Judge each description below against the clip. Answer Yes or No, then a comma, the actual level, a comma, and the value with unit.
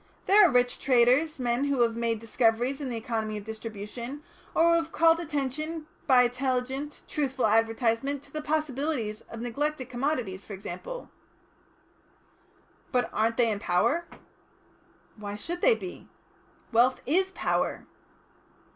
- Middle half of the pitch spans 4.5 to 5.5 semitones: Yes, average, 4.9 semitones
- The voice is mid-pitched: No, very high, 255 Hz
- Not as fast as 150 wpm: Yes, average, 140 wpm